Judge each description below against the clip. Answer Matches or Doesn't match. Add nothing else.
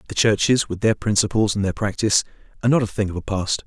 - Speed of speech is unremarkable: Doesn't match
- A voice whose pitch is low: Matches